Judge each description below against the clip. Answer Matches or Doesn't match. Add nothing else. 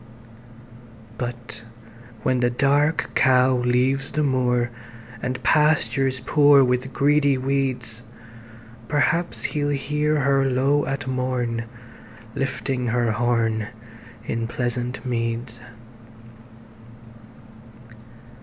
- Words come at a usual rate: Doesn't match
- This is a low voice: Matches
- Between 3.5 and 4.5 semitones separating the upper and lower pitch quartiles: Doesn't match